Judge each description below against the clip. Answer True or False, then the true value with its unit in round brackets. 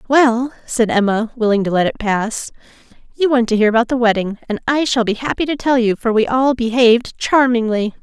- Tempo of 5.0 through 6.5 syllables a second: True (5.5 syllables/s)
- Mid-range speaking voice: False (235 Hz)